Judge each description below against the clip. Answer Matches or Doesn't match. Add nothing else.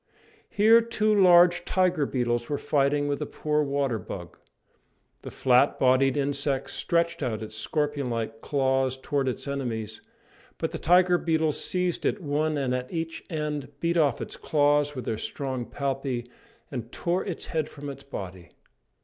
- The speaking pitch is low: Doesn't match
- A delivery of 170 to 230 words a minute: Doesn't match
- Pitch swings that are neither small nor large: Matches